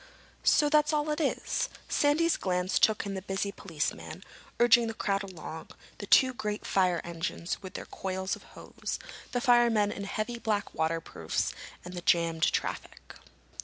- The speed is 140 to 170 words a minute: Yes, average, 160 wpm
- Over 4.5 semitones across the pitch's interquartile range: Yes, average, 5.0 semitones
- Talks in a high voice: Yes, high, 200 Hz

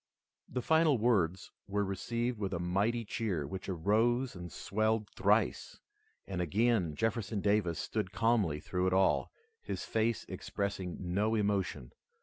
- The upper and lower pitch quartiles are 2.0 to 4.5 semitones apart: Yes, average, 3.6 semitones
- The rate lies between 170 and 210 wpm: No, slow, 135 wpm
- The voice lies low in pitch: Yes, low, 100 Hz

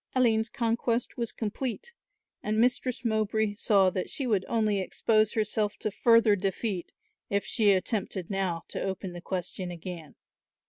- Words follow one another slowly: No, average, 145 wpm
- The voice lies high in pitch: Yes, high, 210 Hz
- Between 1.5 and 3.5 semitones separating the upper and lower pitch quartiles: Yes, average, 3.2 semitones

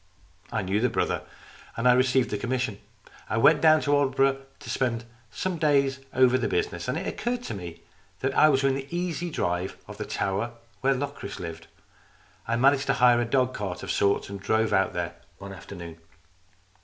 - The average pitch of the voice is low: Yes, low, 125 Hz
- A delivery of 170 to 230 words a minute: Yes, average, 190 wpm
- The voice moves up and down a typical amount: No, wide, 5.7 semitones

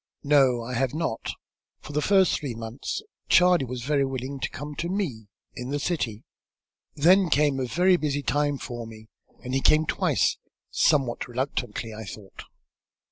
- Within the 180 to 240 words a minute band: No, average, 165 wpm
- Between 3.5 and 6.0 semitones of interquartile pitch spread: Yes, average, 4.0 semitones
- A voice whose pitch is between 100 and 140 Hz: Yes, low, 135 Hz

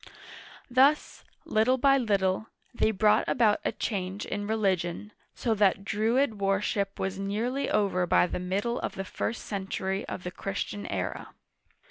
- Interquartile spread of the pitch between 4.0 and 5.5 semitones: No, average, 2.7 semitones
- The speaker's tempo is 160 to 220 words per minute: No, average, 145 wpm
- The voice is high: Yes, high, 205 Hz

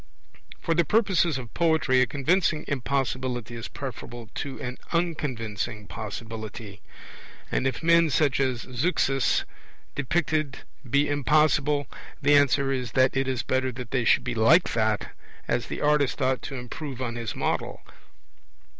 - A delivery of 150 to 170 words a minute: No, average, 140 wpm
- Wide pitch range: No, average, 3.6 semitones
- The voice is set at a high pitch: No, low, 130 Hz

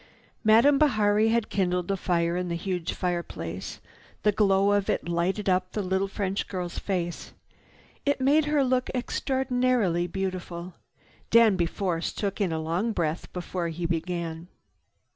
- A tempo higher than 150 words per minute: No, average, 145 wpm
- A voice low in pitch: No, high, 190 Hz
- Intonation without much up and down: No, average, 3.8 semitones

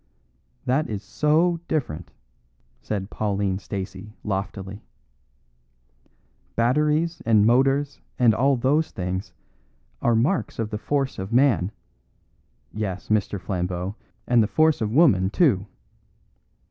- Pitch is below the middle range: Yes, low, 110 Hz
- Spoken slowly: Yes, slow, 110 wpm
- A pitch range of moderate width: No, wide, 6.1 semitones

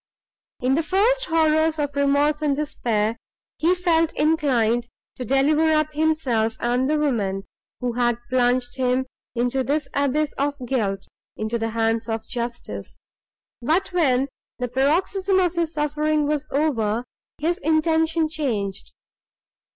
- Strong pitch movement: No, average, 4.5 semitones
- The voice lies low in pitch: No, very high, 280 Hz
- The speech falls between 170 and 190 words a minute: No, slow, 135 wpm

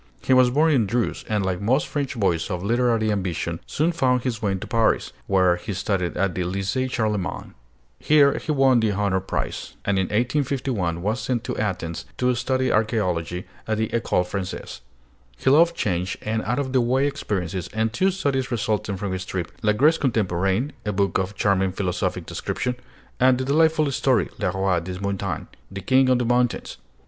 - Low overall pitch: Yes, low, 110 Hz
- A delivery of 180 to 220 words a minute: Yes, average, 185 wpm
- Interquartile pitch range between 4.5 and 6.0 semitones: Yes, average, 5.3 semitones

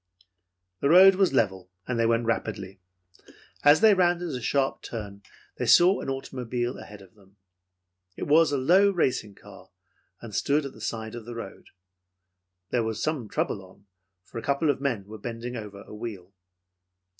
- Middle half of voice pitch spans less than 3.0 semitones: No, average, 5.2 semitones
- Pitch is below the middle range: Yes, low, 120 Hz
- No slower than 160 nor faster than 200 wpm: Yes, average, 175 wpm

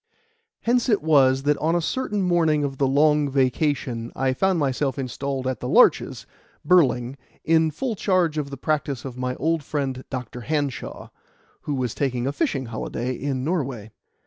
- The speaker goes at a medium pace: Yes, average, 170 wpm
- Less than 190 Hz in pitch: Yes, medium, 140 Hz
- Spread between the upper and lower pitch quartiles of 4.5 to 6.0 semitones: No, average, 3.4 semitones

